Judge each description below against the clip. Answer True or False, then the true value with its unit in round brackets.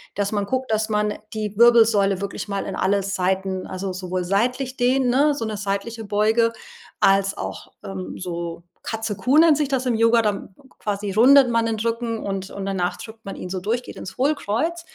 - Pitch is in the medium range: False (215 Hz)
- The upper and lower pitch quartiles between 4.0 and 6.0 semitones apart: False (3.4 semitones)